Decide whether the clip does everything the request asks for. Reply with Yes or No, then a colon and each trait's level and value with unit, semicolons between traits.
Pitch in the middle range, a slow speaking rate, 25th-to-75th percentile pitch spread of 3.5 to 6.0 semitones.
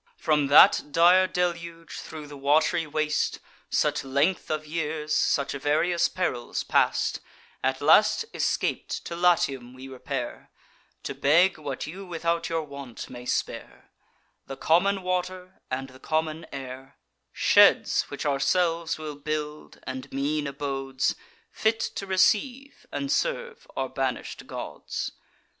Yes: medium, 155 Hz; slow, 130 wpm; average, 4.2 semitones